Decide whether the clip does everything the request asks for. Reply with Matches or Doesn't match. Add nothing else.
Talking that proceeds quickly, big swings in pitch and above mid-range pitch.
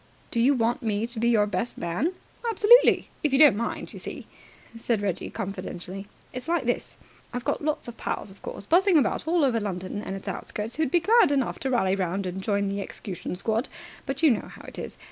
Matches